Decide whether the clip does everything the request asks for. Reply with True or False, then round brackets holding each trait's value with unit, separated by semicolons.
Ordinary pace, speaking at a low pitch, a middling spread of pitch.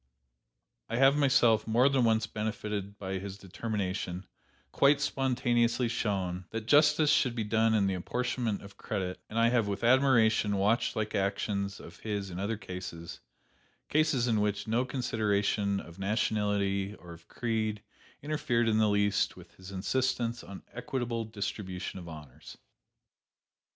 True (145 wpm; 105 Hz; 3.2 semitones)